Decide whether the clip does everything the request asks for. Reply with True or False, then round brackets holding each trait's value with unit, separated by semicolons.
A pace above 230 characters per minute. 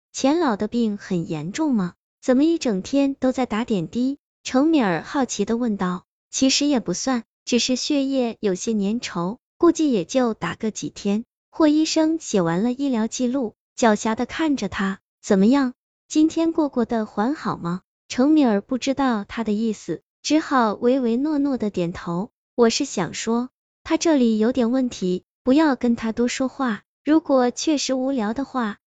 True (245 characters per minute)